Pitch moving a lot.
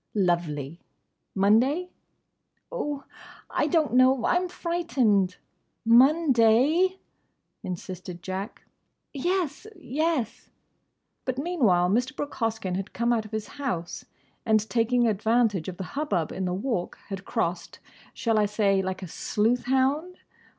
Yes: wide, 6.7 semitones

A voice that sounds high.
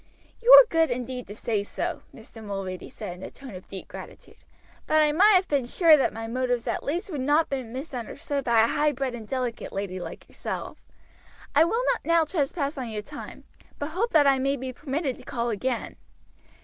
Yes: very high, 265 Hz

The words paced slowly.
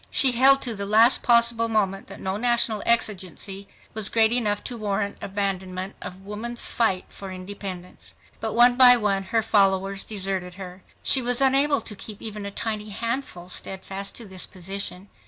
No: average, 170 wpm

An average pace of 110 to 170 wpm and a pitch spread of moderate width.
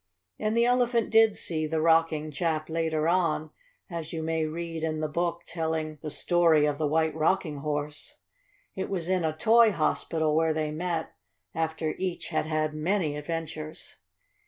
No: average, 165 wpm; narrow, 1.8 semitones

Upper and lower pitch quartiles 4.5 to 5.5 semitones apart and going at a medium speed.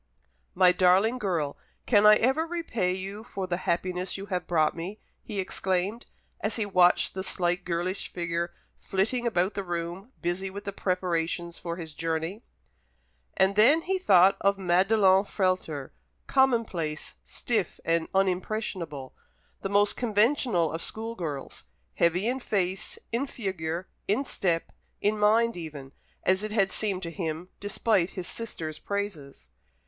No: average, 3.6 semitones; average, 145 wpm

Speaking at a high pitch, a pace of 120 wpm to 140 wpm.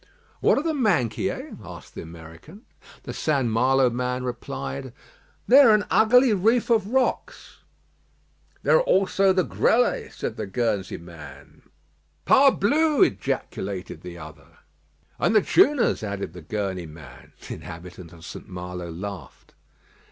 No: low, 120 Hz; slow, 135 wpm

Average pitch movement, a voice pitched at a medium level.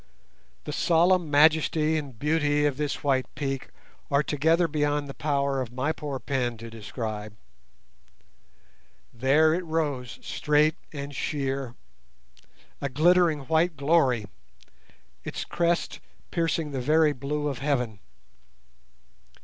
Yes: average, 3.2 semitones; medium, 145 Hz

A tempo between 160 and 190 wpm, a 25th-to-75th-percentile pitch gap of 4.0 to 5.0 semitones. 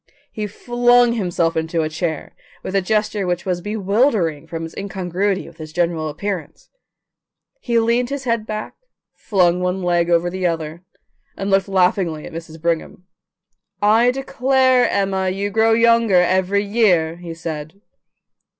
No: average, 150 wpm; average, 4.3 semitones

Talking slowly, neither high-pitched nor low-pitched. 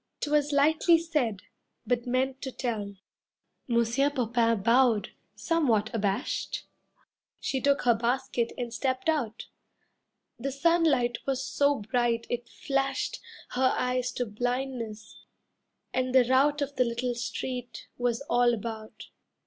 No: slow, 125 wpm; very high, 250 Hz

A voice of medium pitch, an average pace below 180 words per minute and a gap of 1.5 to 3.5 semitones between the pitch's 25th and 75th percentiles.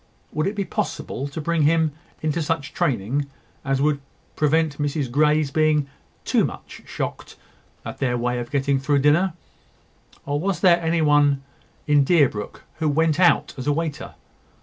Yes: medium, 150 Hz; average, 160 wpm; narrow, 2.6 semitones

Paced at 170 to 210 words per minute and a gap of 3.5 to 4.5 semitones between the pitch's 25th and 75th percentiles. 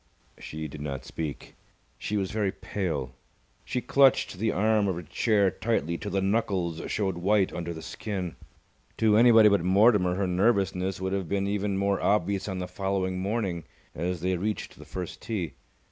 No: average, 175 wpm; average, 2.7 semitones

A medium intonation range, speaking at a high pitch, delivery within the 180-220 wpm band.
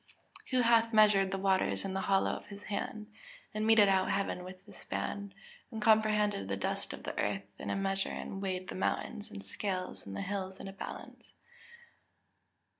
No: narrow, 2.1 semitones; high, 195 Hz; average, 190 wpm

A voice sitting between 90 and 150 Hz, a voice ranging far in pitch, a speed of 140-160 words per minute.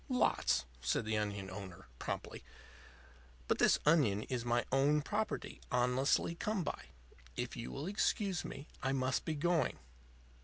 Yes: low, 135 Hz; wide, 7.4 semitones; average, 145 wpm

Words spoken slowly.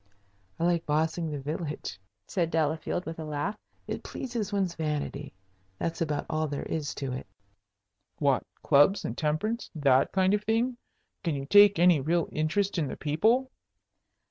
No: average, 160 wpm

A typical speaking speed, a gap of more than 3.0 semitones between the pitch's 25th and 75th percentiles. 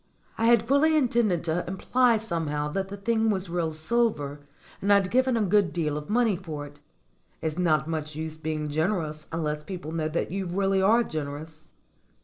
Yes: average, 180 wpm; wide, 5.4 semitones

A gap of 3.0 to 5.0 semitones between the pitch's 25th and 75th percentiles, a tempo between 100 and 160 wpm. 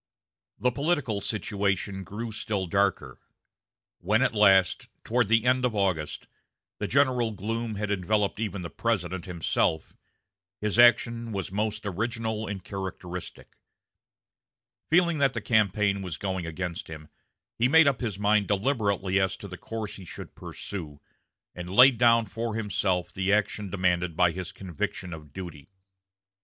Yes: average, 3.5 semitones; average, 145 wpm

